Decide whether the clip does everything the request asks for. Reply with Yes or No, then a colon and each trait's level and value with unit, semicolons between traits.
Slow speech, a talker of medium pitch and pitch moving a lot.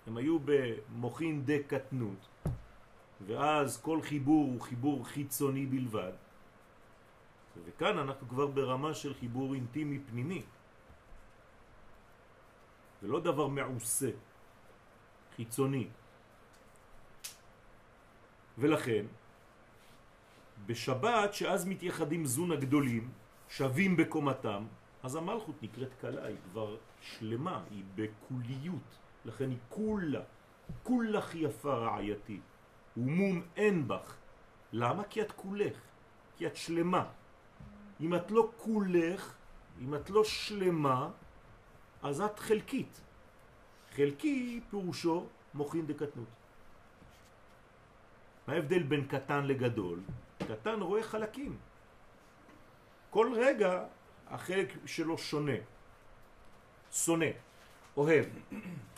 Yes: slow, 90 wpm; medium, 145 Hz; wide, 6.4 semitones